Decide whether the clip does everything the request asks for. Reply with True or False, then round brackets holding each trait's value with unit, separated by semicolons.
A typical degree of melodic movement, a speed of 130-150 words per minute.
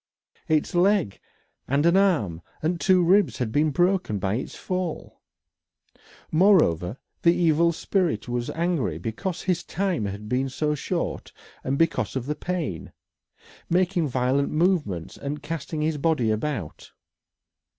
False (6.0 semitones; 135 wpm)